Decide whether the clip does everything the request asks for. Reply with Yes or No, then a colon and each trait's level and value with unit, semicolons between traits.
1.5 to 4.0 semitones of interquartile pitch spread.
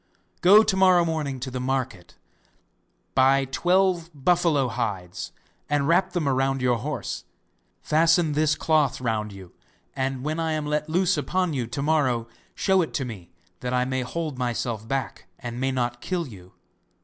No: average, 4.6 semitones